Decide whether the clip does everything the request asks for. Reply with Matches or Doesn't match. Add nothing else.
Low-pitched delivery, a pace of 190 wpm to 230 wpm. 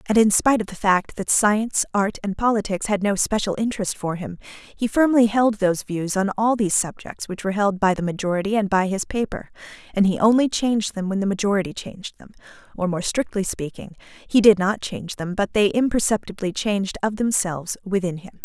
Doesn't match